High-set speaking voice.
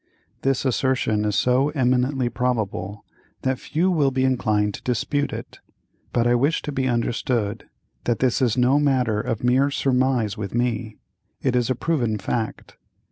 No: low, 125 Hz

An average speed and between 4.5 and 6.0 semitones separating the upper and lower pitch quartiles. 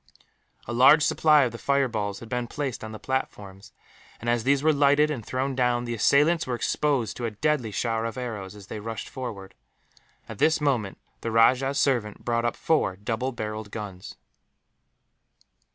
No: average, 175 wpm; average, 4.0 semitones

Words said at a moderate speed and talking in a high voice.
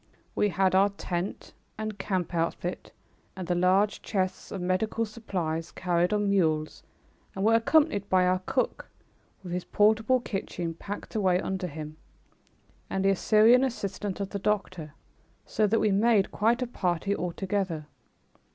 Yes: average, 150 wpm; high, 195 Hz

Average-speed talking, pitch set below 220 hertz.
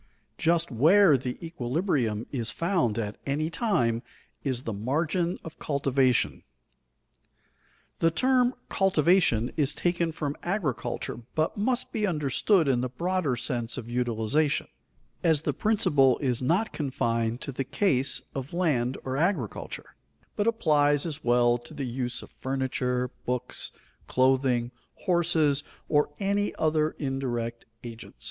No: slow, 130 wpm; medium, 140 Hz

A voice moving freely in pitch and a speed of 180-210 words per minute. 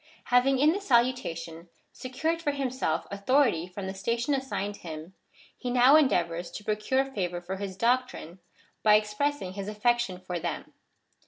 No: wide, 6.1 semitones; average, 150 wpm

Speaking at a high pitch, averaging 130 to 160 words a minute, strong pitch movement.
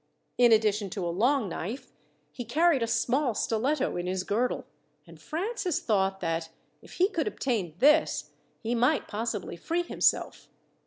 Yes: high, 235 Hz; average, 155 wpm; wide, 6.8 semitones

